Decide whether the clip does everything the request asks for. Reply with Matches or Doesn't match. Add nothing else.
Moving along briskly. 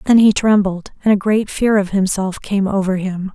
Matches